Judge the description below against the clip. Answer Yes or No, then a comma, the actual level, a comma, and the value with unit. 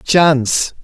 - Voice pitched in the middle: Yes, medium, 145 Hz